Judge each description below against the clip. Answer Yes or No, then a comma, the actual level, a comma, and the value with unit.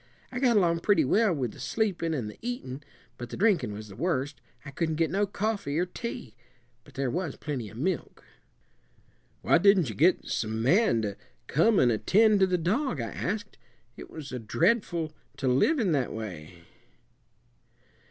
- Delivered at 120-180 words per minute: Yes, average, 175 wpm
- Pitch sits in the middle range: Yes, medium, 165 Hz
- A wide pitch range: Yes, wide, 8.1 semitones